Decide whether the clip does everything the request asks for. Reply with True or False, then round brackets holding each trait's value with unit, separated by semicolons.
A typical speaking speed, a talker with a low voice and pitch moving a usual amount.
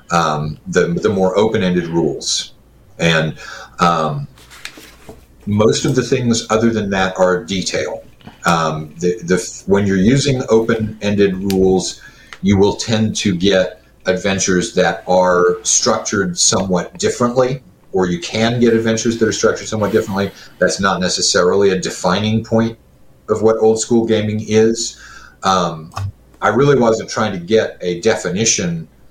True (145 wpm; 100 Hz; 3.8 semitones)